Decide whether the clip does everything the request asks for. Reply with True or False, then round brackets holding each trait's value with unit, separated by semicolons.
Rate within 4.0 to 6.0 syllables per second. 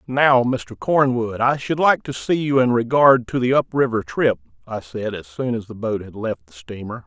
True (4.7 syllables/s)